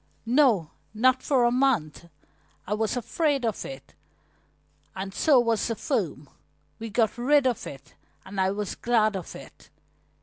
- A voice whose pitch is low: No, high, 225 Hz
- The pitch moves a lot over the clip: No, average, 4.8 semitones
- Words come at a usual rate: Yes, average, 155 wpm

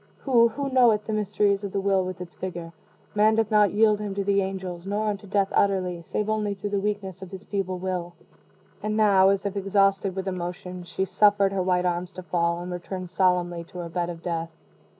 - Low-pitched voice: No, high, 195 Hz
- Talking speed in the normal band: No, fast, 215 wpm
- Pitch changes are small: Yes, narrow, 2.3 semitones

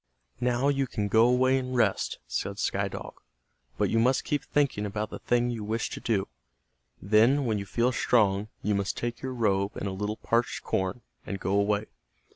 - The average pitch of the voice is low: Yes, low, 115 Hz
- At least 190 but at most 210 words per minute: Yes, average, 195 wpm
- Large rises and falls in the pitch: No, average, 3.4 semitones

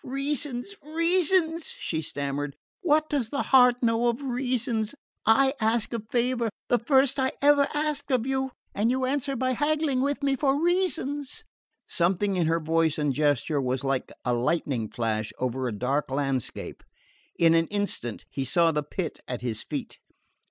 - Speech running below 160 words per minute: No, average, 165 wpm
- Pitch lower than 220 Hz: No, high, 235 Hz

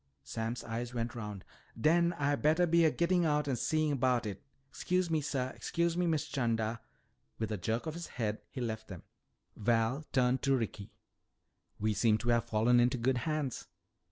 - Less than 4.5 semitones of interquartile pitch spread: No, wide, 5.4 semitones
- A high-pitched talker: No, low, 125 Hz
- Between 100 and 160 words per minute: No, average, 185 wpm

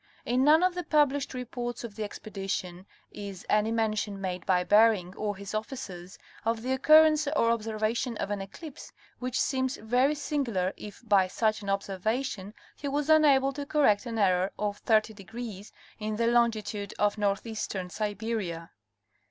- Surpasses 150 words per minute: Yes, average, 160 wpm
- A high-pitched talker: Yes, high, 220 Hz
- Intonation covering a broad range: No, average, 4.2 semitones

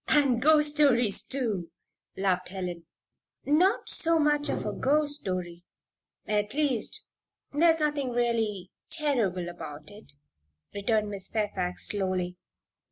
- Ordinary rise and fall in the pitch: No, wide, 7.9 semitones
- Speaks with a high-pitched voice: Yes, high, 220 Hz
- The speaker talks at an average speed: No, slow, 115 wpm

